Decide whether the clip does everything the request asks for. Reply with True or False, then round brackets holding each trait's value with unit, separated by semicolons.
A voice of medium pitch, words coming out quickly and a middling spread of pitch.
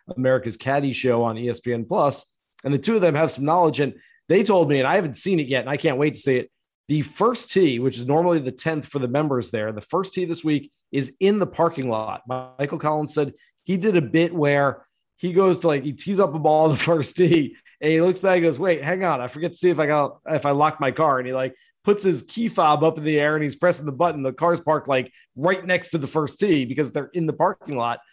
True (155 Hz; 270 wpm; 4.1 semitones)